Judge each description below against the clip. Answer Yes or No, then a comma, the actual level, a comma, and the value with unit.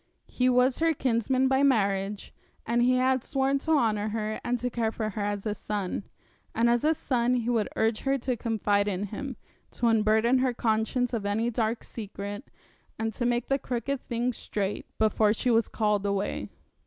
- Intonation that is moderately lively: Yes, average, 3.0 semitones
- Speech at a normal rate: Yes, average, 190 wpm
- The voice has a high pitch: Yes, high, 230 Hz